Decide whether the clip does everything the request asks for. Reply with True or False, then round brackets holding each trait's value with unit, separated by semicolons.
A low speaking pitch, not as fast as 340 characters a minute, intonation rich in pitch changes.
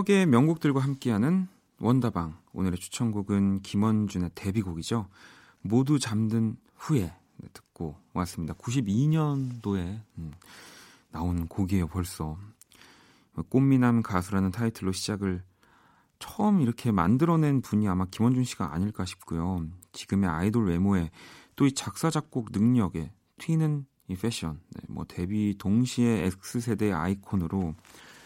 False (105 Hz; 270 characters per minute; 5.0 semitones)